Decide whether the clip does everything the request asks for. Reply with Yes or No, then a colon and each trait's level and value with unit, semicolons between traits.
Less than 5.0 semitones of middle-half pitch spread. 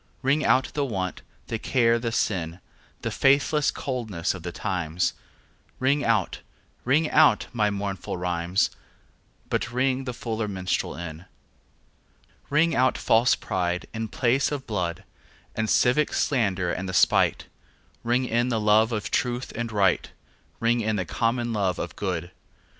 No: average, 5.3 semitones